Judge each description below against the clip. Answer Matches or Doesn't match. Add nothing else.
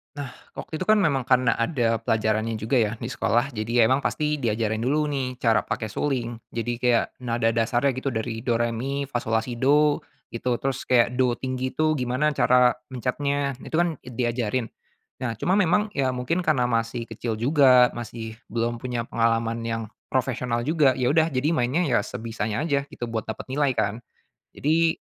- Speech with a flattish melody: Doesn't match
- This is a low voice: Matches